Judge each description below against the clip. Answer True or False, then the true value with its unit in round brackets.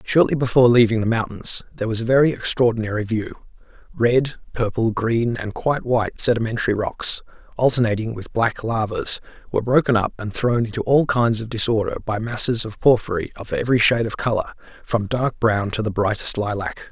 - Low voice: True (115 Hz)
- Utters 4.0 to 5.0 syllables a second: False (5.6 syllables/s)